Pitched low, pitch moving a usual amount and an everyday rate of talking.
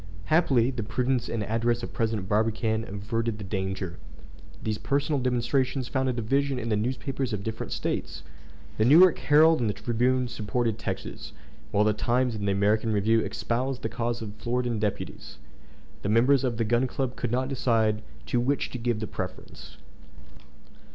Yes: low, 115 Hz; average, 3.0 semitones; average, 180 wpm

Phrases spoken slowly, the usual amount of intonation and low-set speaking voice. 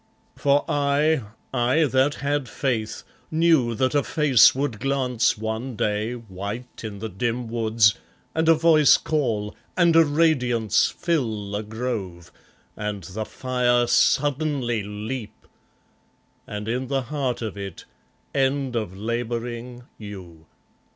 Yes: slow, 125 wpm; average, 4.4 semitones; low, 120 Hz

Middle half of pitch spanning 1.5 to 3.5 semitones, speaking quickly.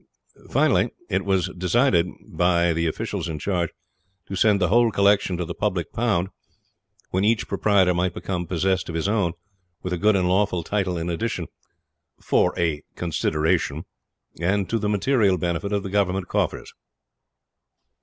No: average, 2.8 semitones; average, 155 wpm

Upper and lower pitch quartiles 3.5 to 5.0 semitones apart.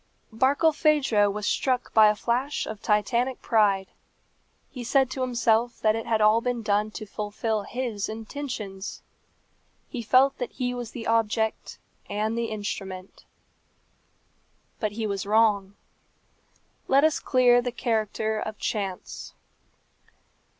No: average, 2.8 semitones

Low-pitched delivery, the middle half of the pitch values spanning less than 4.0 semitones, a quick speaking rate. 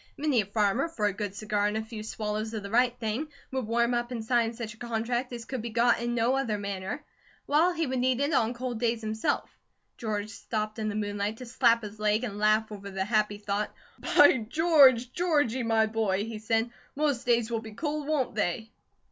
No: high, 225 Hz; average, 2.7 semitones; fast, 215 wpm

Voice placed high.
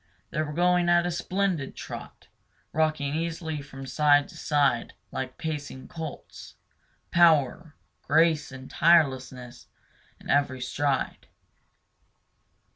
No: medium, 150 Hz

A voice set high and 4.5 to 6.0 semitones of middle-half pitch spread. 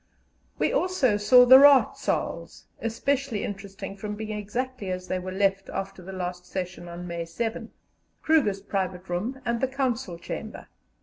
Yes: high, 205 Hz; average, 5.2 semitones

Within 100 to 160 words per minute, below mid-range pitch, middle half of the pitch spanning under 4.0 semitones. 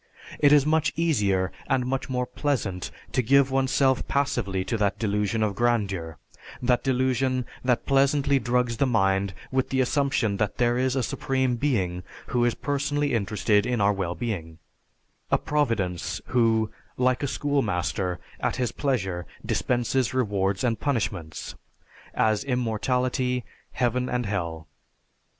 No: average, 140 wpm; low, 120 Hz; average, 4.5 semitones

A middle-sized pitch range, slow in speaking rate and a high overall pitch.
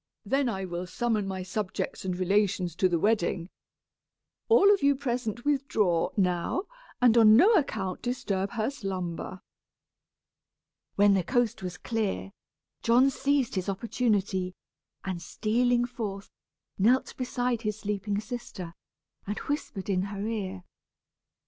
Yes: average, 4.5 semitones; slow, 130 wpm; high, 210 Hz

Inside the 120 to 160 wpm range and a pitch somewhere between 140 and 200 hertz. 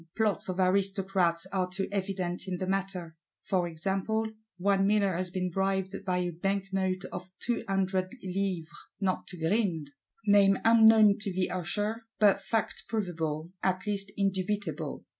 Yes: average, 140 wpm; high, 190 Hz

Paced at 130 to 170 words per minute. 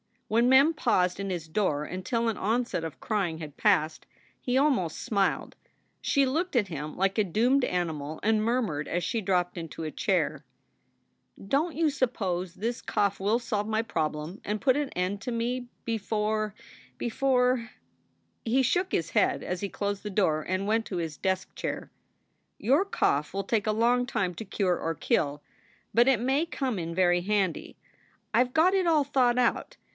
No: average, 180 wpm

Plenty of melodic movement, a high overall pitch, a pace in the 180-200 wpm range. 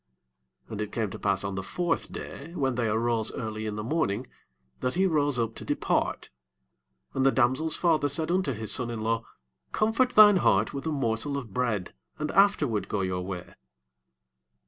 No: wide, 6.5 semitones; low, 120 Hz; average, 190 wpm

